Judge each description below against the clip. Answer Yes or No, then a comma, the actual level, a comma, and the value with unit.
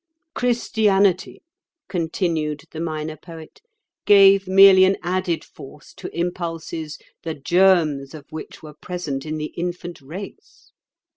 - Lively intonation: No, average, 3.3 semitones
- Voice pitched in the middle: Yes, medium, 170 Hz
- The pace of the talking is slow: Yes, slow, 120 wpm